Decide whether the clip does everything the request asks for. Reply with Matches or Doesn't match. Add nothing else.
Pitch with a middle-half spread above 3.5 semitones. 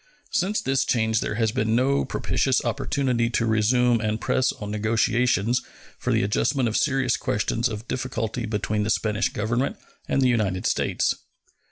Doesn't match